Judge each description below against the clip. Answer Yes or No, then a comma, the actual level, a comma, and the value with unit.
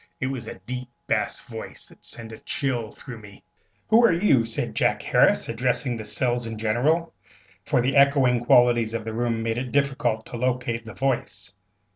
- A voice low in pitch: Yes, low, 120 Hz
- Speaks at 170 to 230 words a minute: Yes, average, 185 wpm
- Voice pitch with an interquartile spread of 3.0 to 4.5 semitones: No, narrow, 2.6 semitones